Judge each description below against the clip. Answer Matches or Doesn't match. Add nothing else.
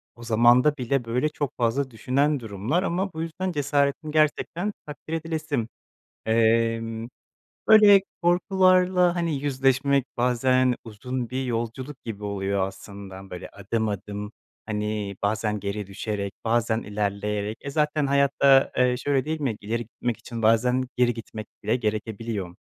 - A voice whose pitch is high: Doesn't match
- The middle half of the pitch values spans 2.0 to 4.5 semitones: Doesn't match